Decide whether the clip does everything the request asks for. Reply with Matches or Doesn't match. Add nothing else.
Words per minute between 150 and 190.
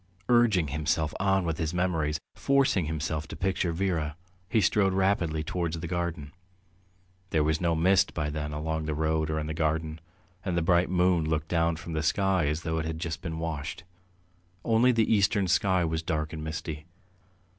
Matches